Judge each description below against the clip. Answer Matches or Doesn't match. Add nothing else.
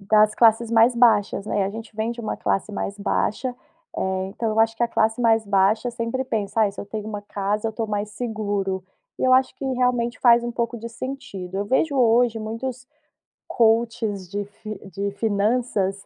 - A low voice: Doesn't match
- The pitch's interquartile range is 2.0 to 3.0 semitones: Matches